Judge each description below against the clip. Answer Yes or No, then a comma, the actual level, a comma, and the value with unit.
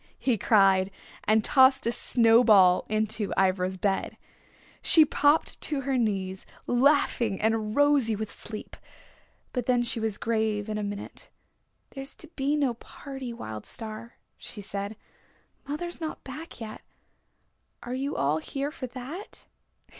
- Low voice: No, high, 230 Hz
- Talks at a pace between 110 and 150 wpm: Yes, average, 140 wpm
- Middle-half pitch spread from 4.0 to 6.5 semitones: Yes, average, 4.6 semitones